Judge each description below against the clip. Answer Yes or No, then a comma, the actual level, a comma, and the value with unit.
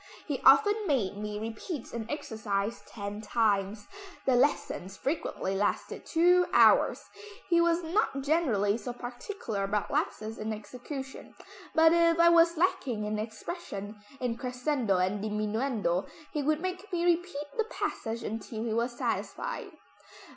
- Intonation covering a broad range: Yes, wide, 7.7 semitones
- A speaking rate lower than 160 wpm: Yes, average, 140 wpm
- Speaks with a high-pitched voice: Yes, high, 245 Hz